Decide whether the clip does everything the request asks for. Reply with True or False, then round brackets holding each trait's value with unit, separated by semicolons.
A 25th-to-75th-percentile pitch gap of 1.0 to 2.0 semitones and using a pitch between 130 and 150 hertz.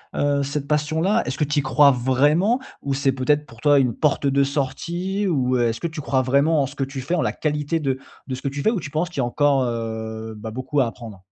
False (2.8 semitones; 140 Hz)